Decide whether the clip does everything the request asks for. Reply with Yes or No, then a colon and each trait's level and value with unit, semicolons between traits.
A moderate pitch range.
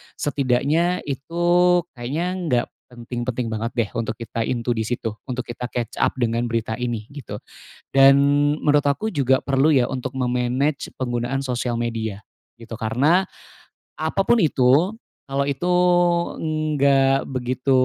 Yes: average, 3.1 semitones